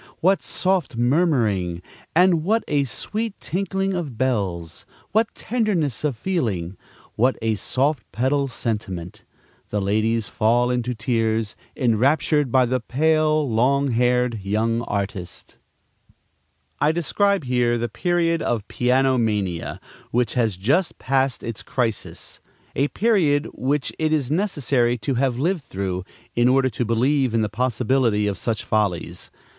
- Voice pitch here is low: Yes, low, 125 Hz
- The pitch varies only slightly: No, average, 5.2 semitones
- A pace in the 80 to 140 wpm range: Yes, slow, 135 wpm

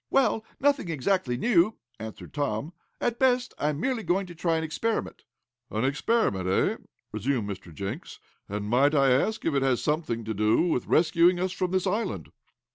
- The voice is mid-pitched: Yes, medium, 155 Hz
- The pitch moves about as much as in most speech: No, wide, 8.1 semitones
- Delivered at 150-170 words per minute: No, average, 180 wpm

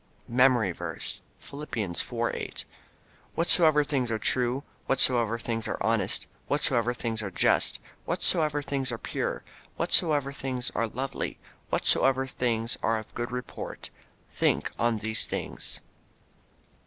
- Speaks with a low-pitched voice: Yes, low, 125 Hz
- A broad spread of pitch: No, average, 3.2 semitones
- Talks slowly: Yes, slow, 125 wpm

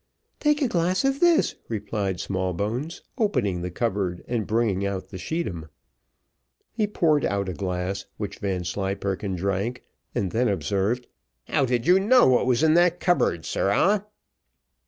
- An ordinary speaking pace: Yes, average, 145 wpm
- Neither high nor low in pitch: No, low, 105 Hz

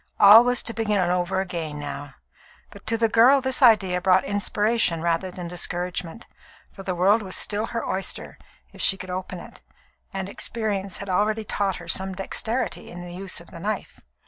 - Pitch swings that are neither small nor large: Yes, average, 3.3 semitones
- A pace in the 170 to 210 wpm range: Yes, average, 185 wpm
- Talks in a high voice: Yes, high, 195 Hz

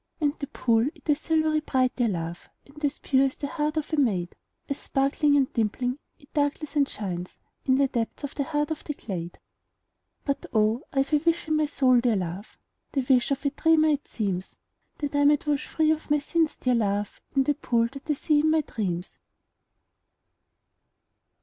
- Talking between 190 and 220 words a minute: Yes, average, 200 wpm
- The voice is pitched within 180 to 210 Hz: No, very high, 275 Hz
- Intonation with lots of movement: No, average, 4.4 semitones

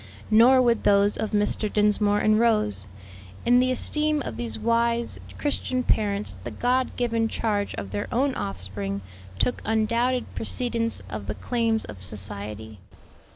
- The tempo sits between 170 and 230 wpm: No, average, 145 wpm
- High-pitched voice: Yes, high, 215 Hz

